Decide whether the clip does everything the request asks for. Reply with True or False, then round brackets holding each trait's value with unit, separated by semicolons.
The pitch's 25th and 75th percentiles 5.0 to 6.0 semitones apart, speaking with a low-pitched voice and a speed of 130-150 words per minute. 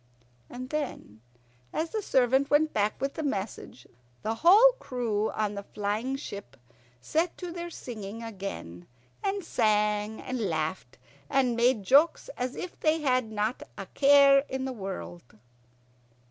False (5.5 semitones; 245 Hz; 145 wpm)